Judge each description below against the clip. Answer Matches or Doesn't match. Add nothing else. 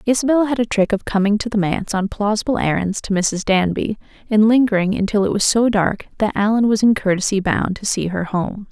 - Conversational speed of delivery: Doesn't match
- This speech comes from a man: Doesn't match